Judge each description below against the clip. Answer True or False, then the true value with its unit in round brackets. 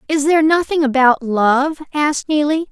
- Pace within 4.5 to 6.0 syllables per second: True (4.9 syllables/s)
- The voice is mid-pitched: False (290 Hz)